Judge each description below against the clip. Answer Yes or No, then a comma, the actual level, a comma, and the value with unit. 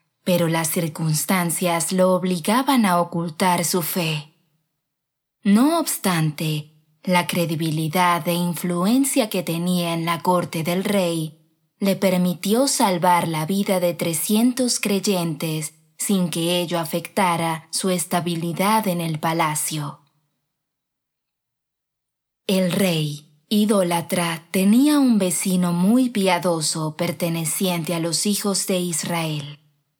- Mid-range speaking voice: Yes, medium, 175 Hz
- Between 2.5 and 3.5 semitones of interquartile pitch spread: Yes, average, 3.0 semitones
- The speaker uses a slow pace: Yes, slow, 105 wpm